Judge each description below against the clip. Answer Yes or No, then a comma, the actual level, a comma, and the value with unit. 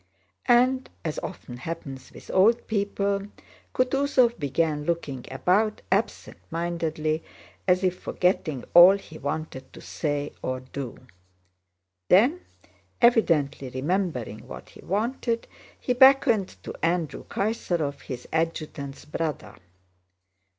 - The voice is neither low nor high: Yes, medium, 170 Hz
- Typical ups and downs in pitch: No, wide, 6.3 semitones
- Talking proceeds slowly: Yes, slow, 110 wpm